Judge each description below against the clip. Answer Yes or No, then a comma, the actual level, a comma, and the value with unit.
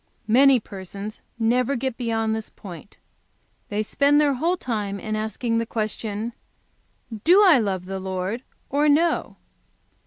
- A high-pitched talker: Yes, high, 225 Hz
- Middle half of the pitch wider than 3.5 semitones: Yes, average, 4.5 semitones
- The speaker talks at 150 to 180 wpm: No, slow, 135 wpm